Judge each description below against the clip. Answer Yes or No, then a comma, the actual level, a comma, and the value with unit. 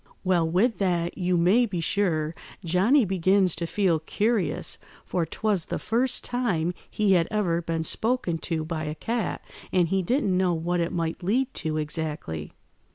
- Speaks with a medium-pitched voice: Yes, medium, 180 Hz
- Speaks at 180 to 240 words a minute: No, average, 165 wpm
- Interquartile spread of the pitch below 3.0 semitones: No, average, 3.9 semitones